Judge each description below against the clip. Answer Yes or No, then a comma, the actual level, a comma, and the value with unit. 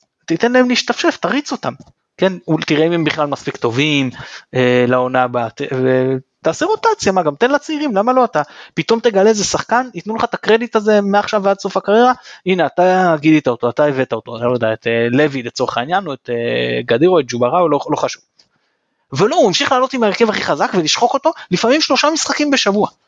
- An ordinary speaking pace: No, fast, 195 wpm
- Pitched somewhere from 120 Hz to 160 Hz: No, medium, 185 Hz